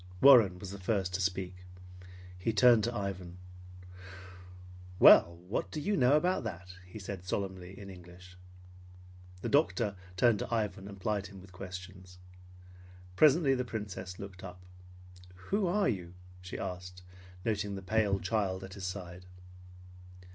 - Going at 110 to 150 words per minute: Yes, average, 145 wpm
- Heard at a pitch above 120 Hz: No, very low, 95 Hz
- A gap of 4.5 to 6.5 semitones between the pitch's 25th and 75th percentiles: No, average, 3.3 semitones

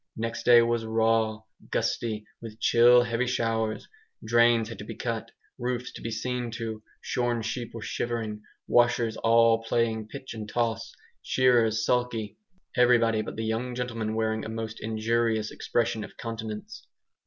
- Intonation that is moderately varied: No, narrow, 1.2 semitones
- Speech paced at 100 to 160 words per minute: Yes, average, 150 wpm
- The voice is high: No, low, 115 Hz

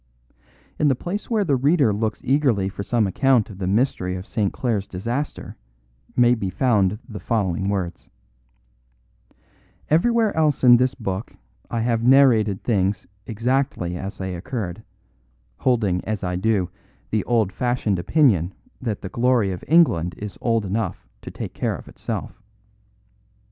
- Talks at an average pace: Yes, average, 150 wpm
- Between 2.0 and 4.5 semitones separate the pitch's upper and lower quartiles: No, average, 5.0 semitones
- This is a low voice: Yes, low, 110 Hz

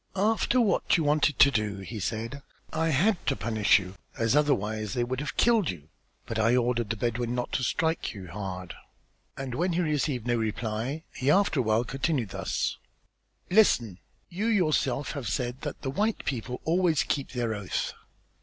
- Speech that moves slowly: No, average, 180 wpm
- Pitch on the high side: No, low, 125 Hz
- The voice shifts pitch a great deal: Yes, wide, 6.0 semitones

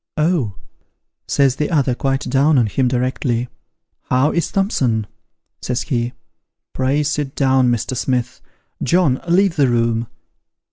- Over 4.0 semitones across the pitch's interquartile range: No, average, 3.2 semitones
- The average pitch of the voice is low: Yes, low, 130 Hz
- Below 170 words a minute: Yes, average, 145 wpm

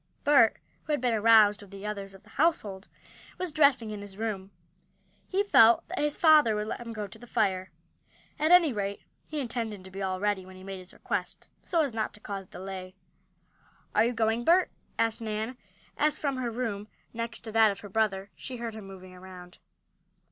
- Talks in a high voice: Yes, high, 220 Hz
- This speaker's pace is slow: No, fast, 205 wpm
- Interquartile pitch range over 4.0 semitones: No, average, 3.7 semitones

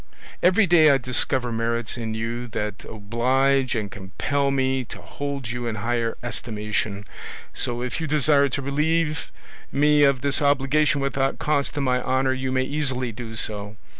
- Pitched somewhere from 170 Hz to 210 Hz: No, low, 130 Hz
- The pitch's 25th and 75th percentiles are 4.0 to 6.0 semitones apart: No, average, 3.5 semitones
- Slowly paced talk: No, average, 165 wpm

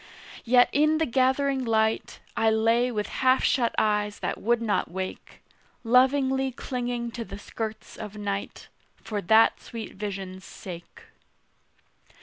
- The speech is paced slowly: Yes, slow, 130 wpm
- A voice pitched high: Yes, high, 230 Hz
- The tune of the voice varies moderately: Yes, average, 3.5 semitones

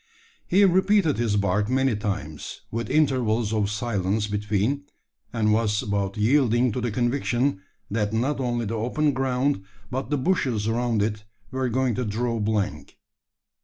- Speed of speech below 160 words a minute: Yes, average, 150 wpm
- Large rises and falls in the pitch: No, average, 4.0 semitones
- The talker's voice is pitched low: Yes, low, 115 Hz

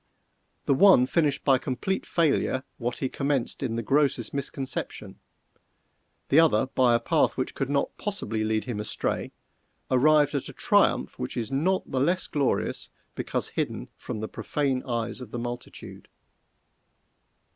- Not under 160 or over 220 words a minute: No, average, 150 wpm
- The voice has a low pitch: Yes, low, 130 Hz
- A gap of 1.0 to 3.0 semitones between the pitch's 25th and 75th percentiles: No, average, 3.5 semitones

